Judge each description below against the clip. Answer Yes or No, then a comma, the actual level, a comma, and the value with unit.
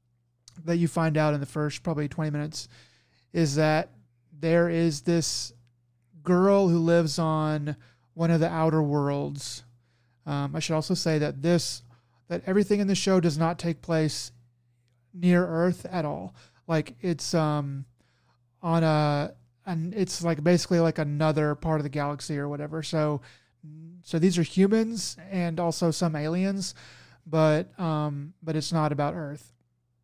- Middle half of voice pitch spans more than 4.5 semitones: No, average, 3.3 semitones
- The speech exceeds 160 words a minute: No, average, 155 wpm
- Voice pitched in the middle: Yes, medium, 155 Hz